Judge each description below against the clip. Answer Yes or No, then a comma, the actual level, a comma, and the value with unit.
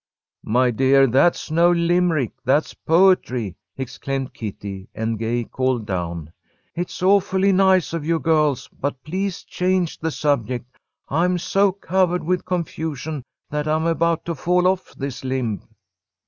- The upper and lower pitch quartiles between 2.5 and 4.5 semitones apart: No, wide, 5.6 semitones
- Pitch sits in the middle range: Yes, medium, 155 Hz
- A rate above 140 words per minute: No, slow, 135 wpm